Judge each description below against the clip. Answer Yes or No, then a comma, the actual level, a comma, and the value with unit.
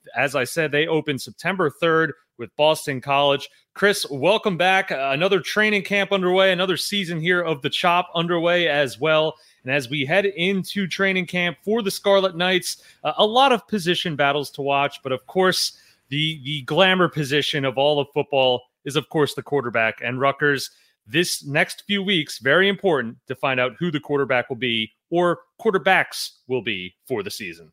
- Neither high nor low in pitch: Yes, medium, 155 Hz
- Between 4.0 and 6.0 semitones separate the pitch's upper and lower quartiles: Yes, average, 5.0 semitones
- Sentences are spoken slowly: No, average, 180 wpm